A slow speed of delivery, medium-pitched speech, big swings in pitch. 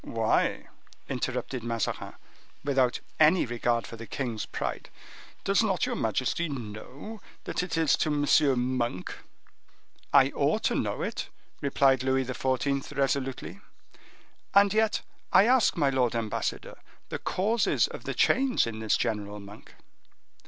No: slow, 130 wpm; low, 130 Hz; wide, 5.9 semitones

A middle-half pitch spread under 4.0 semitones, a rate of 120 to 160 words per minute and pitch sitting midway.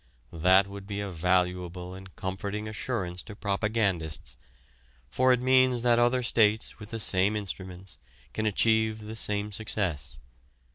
No: average, 3.1 semitones; average, 140 wpm; low, 100 Hz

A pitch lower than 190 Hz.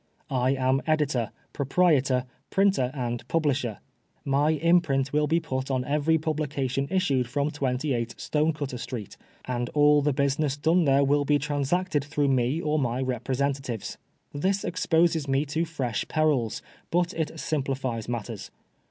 Yes: medium, 140 Hz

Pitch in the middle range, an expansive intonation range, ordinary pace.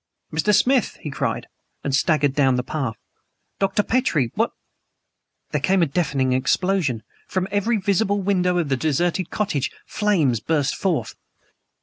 Yes: medium, 165 Hz; wide, 6.0 semitones; average, 145 wpm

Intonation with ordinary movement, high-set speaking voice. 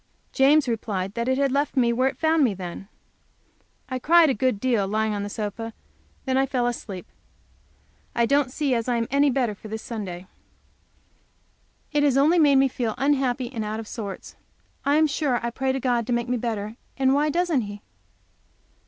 Yes: average, 4.0 semitones; very high, 250 Hz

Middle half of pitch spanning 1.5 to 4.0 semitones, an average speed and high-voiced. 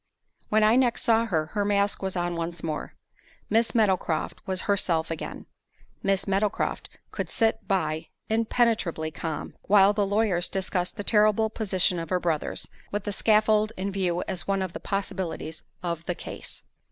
Yes: average, 3.4 semitones; average, 165 wpm; high, 195 Hz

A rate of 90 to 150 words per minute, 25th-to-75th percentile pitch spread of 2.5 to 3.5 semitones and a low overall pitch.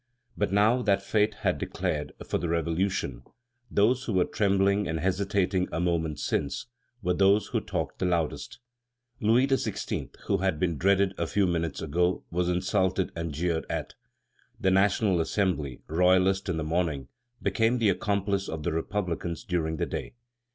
No: average, 160 wpm; average, 3.2 semitones; very low, 90 Hz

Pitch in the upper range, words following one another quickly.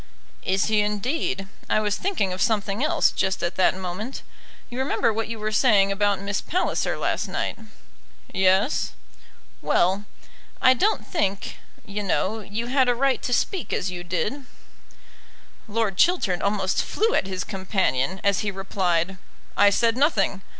No: high, 205 Hz; average, 155 wpm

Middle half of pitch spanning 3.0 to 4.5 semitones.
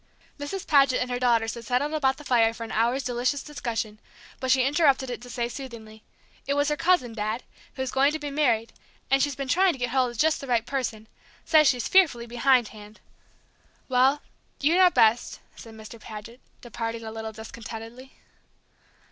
Yes: average, 3.5 semitones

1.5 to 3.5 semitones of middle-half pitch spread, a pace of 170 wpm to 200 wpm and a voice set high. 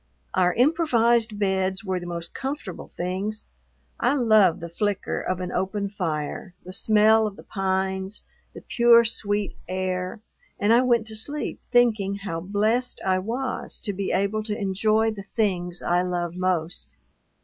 No: average, 3.1 semitones; average, 155 wpm; high, 200 Hz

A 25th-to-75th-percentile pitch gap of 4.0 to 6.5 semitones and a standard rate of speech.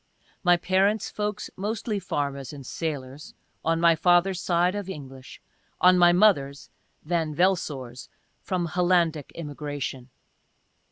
No: average, 4.4 semitones; slow, 125 wpm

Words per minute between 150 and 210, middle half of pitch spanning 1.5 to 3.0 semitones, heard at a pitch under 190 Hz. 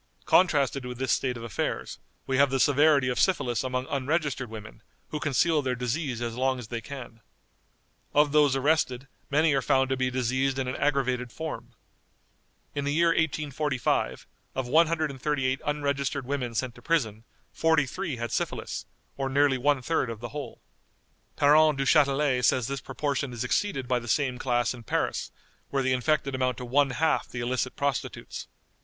Yes: average, 170 wpm; average, 2.7 semitones; low, 135 Hz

